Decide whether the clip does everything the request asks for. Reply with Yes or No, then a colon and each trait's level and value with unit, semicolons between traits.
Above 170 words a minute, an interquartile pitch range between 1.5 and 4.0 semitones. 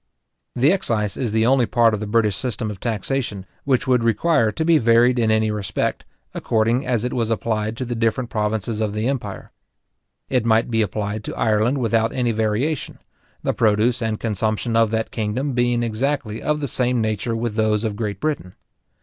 Yes: average, 190 wpm; narrow, 2.4 semitones